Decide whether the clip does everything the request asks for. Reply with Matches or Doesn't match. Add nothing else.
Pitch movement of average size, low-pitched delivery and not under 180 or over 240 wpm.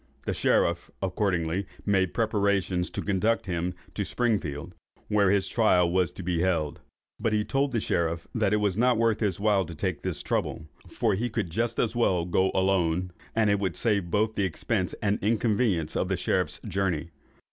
Matches